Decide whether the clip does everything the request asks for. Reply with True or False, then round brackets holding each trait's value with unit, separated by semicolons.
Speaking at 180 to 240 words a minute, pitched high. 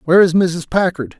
False (200 wpm; 170 Hz)